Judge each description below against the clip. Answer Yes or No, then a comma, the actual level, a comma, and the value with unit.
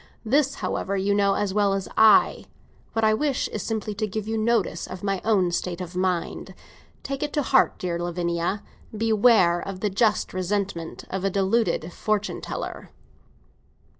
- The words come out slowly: No, average, 165 wpm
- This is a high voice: Yes, high, 200 Hz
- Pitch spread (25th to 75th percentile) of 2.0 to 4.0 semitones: Yes, average, 3.0 semitones